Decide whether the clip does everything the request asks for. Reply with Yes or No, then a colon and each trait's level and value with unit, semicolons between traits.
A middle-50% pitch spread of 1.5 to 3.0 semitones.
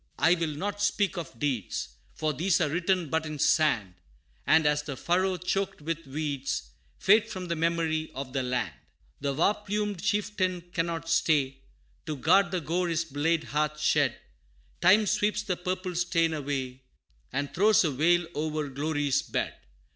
No: average, 3.9 semitones